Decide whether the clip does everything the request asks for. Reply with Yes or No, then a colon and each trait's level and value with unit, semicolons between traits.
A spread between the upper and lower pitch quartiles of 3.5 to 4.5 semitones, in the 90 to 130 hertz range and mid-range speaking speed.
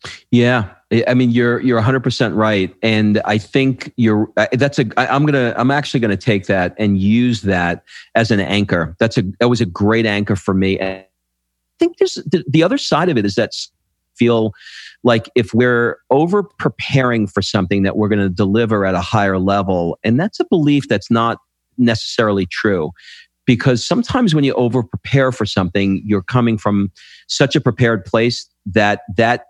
Yes: average, 3.9 semitones; low, 115 Hz; average, 185 wpm